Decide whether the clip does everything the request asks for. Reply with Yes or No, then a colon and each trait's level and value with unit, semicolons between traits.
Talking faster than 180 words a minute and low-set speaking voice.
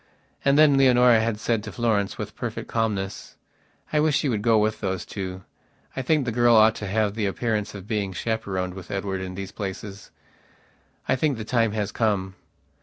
Yes: average, 190 wpm; low, 110 Hz